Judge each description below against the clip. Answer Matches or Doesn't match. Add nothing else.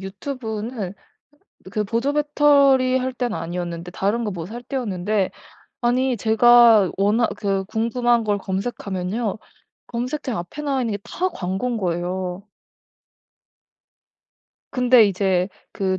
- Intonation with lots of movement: Doesn't match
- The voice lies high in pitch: Matches